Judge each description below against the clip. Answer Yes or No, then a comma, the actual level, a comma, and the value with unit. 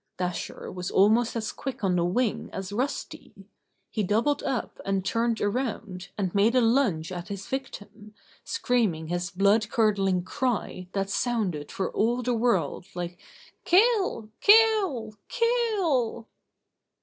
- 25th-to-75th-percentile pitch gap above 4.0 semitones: Yes, average, 4.7 semitones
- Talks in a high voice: Yes, high, 220 Hz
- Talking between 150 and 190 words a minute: No, slow, 135 wpm